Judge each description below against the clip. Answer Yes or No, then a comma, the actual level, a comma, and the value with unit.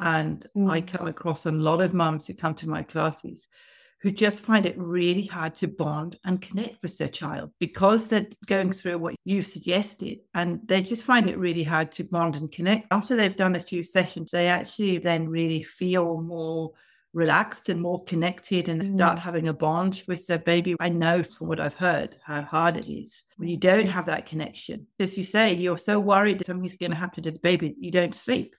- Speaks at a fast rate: Yes, fast, 210 wpm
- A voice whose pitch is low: No, medium, 175 Hz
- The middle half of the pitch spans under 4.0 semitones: Yes, narrow, 2.5 semitones